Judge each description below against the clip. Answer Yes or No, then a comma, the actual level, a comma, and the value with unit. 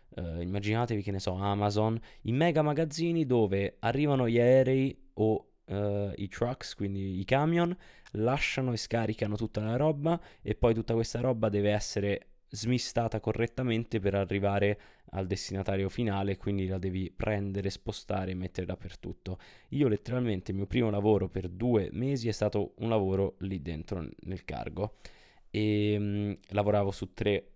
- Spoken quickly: No, average, 150 wpm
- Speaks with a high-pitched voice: No, low, 105 Hz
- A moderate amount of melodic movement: Yes, average, 3.2 semitones